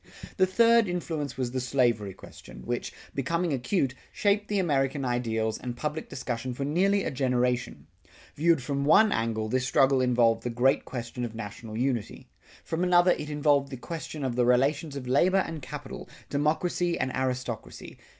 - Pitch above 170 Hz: No, low, 135 Hz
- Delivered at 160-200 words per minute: Yes, average, 165 wpm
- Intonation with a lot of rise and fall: No, average, 4.7 semitones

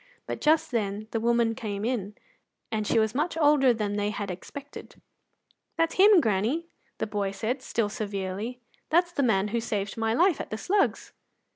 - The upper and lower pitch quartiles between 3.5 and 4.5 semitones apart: No, average, 5.3 semitones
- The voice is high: Yes, high, 225 Hz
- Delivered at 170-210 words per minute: Yes, average, 175 wpm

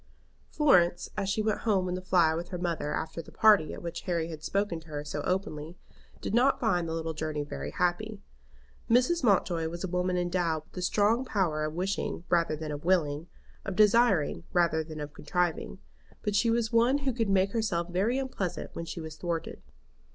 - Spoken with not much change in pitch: No, average, 4.3 semitones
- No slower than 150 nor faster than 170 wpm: No, average, 200 wpm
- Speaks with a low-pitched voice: No, medium, 180 Hz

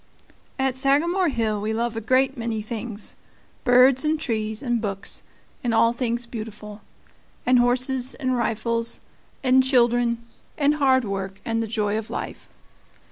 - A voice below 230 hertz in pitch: No, high, 235 Hz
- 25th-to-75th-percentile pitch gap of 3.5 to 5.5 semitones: No, average, 2.9 semitones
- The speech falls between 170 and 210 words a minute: No, average, 145 wpm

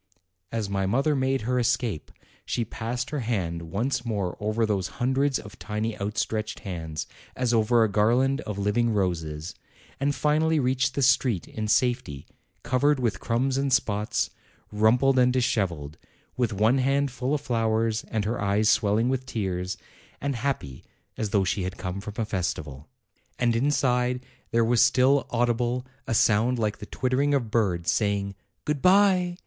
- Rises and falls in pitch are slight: No, average, 4.0 semitones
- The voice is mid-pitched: No, low, 115 Hz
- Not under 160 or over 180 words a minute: Yes, average, 165 wpm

